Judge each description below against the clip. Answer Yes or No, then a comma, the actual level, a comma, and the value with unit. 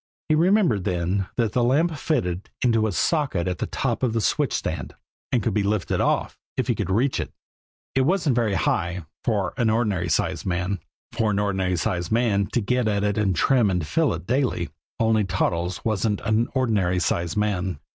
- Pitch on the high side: No, low, 105 Hz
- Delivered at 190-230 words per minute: Yes, average, 195 wpm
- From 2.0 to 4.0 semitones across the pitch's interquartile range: No, average, 4.7 semitones